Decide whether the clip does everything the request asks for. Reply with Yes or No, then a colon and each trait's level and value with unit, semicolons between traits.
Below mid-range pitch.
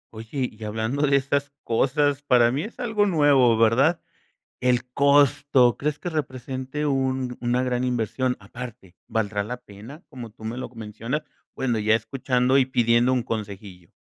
Yes: low, 125 Hz